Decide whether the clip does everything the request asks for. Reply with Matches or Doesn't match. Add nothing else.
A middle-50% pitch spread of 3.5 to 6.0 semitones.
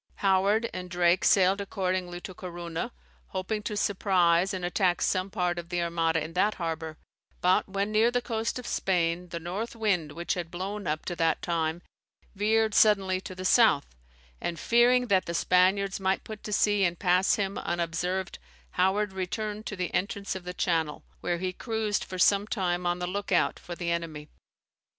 Doesn't match